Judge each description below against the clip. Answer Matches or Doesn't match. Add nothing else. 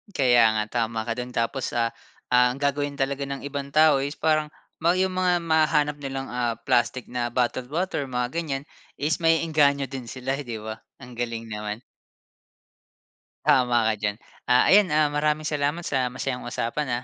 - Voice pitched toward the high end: Doesn't match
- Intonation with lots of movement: Doesn't match